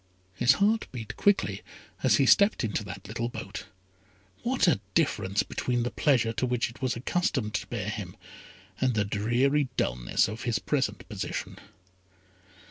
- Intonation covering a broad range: No, average, 4.5 semitones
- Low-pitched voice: Yes, low, 120 Hz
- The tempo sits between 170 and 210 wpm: No, average, 155 wpm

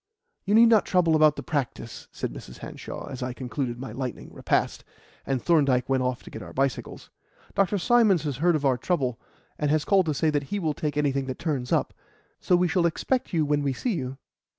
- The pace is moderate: No, fast, 220 wpm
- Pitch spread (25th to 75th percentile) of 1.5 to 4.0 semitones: No, average, 4.8 semitones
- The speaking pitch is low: No, medium, 145 Hz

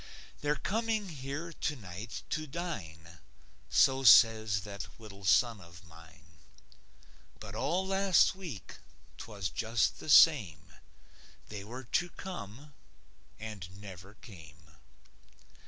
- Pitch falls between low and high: No, low, 110 Hz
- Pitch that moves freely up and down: Yes, wide, 8.5 semitones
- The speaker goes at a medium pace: No, slow, 105 wpm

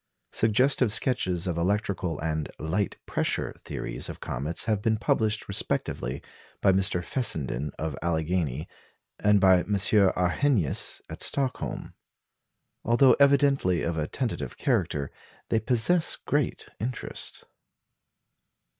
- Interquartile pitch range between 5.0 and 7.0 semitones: Yes, wide, 5.5 semitones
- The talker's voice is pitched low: Yes, very low, 95 Hz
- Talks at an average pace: No, slow, 110 wpm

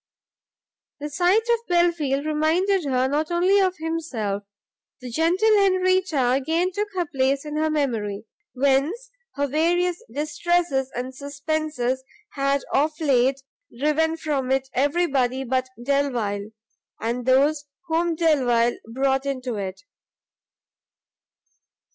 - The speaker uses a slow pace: Yes, slow, 115 wpm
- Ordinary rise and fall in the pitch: Yes, average, 4.4 semitones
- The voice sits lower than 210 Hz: No, very high, 285 Hz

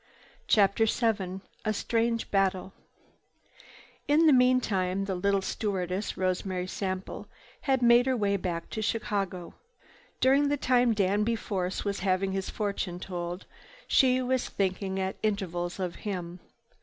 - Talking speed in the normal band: No, slow, 130 wpm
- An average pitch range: Yes, average, 3.6 semitones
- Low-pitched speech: No, high, 200 Hz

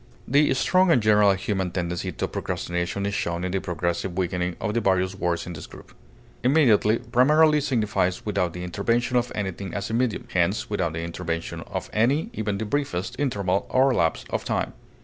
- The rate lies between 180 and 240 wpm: Yes, average, 185 wpm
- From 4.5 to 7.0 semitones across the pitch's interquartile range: Yes, average, 5.2 semitones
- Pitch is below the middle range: Yes, low, 100 Hz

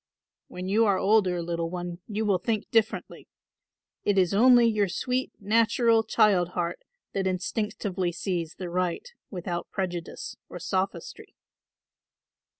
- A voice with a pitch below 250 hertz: Yes, high, 190 Hz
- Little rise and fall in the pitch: No, average, 3.6 semitones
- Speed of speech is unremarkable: No, slow, 130 wpm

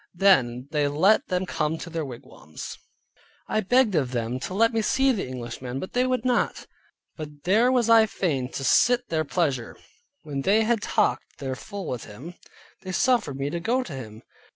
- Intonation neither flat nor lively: No, wide, 8.7 semitones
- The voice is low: No, medium, 170 Hz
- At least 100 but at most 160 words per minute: No, average, 190 wpm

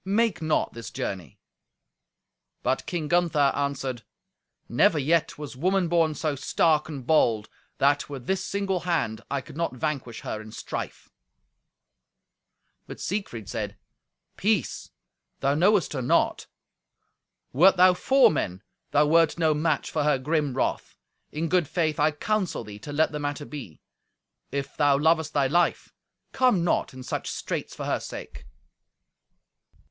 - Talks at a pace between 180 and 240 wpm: No, average, 145 wpm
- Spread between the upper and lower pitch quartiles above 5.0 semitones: No, average, 4.2 semitones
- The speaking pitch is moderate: Yes, medium, 150 Hz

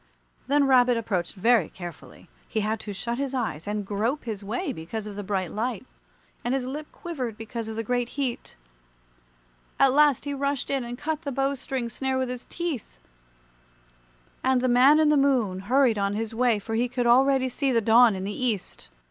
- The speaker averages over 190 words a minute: Yes, average, 200 wpm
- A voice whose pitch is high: Yes, high, 245 Hz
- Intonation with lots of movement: No, average, 3.9 semitones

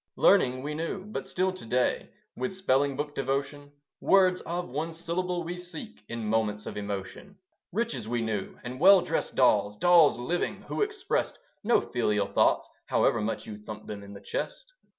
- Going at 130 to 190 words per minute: Yes, average, 170 wpm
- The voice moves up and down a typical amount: No, wide, 8.0 semitones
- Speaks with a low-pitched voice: No, medium, 145 Hz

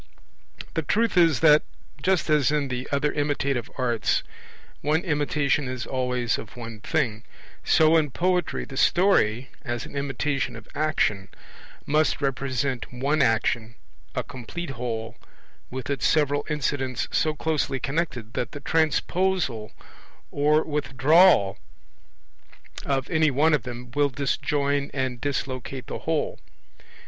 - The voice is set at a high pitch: No, medium, 140 Hz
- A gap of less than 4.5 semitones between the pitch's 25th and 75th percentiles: Yes, average, 3.4 semitones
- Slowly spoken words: Yes, slow, 130 wpm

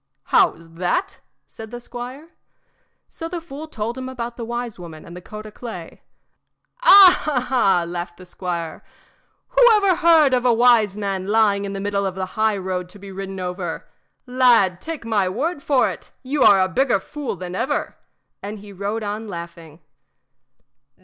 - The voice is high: Yes, high, 215 Hz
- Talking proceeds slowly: No, average, 170 wpm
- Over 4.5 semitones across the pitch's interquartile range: Yes, wide, 5.5 semitones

